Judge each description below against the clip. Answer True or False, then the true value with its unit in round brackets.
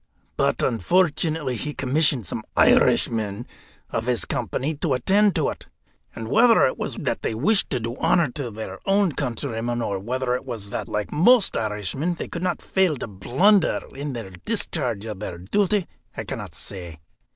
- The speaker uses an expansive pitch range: True (7.3 semitones)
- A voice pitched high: False (125 Hz)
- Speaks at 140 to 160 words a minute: False (175 wpm)